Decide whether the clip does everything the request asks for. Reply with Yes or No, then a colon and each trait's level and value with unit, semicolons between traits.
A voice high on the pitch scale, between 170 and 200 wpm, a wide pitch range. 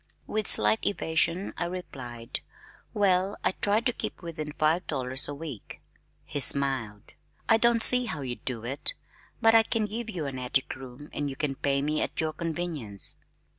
No: medium, 155 Hz; average, 175 wpm; wide, 6.1 semitones